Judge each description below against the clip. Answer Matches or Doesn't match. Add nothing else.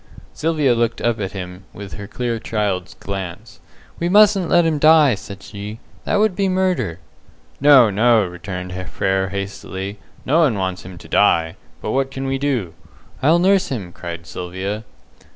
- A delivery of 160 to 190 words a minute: Matches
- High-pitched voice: Doesn't match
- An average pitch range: Doesn't match